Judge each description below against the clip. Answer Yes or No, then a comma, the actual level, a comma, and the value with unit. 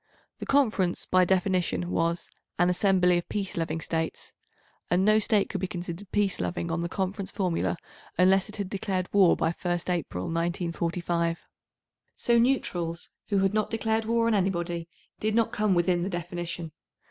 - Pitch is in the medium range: Yes, medium, 180 Hz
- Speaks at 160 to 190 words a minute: Yes, average, 165 wpm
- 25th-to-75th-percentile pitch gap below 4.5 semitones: Yes, average, 2.9 semitones